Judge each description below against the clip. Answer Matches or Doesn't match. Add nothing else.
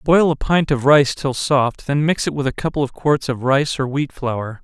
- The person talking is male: Matches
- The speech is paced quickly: Matches